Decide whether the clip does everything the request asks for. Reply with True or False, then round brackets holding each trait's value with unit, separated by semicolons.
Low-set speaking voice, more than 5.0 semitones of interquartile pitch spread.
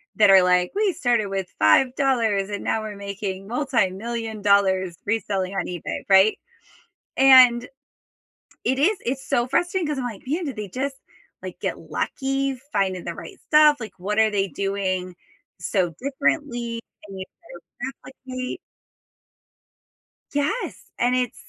False (225 Hz; 5.4 semitones)